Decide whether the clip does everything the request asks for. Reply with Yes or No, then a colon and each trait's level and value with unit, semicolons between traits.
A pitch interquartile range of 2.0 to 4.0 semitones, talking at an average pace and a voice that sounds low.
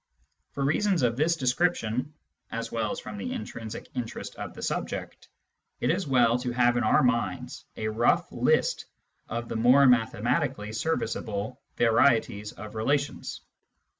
Yes: average, 3.6 semitones; average, 145 wpm; low, 120 Hz